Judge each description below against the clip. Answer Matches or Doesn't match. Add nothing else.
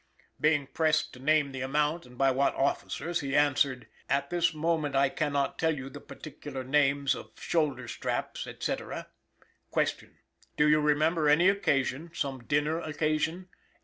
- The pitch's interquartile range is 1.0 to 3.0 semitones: Matches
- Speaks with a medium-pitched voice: Matches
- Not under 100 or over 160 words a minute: Matches